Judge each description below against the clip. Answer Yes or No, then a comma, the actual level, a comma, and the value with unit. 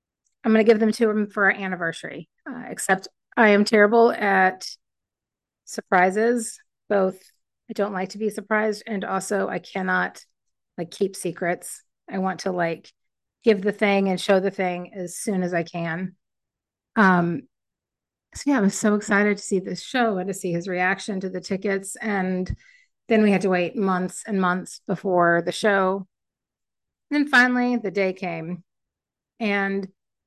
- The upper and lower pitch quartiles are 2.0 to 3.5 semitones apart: Yes, average, 2.8 semitones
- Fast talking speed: No, average, 170 wpm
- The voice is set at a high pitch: Yes, high, 195 Hz